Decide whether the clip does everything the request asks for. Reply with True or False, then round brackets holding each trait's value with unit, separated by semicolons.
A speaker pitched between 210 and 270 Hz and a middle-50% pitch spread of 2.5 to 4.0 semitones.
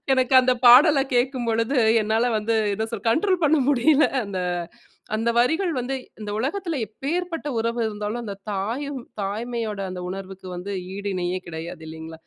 False (230 Hz; 5.2 semitones)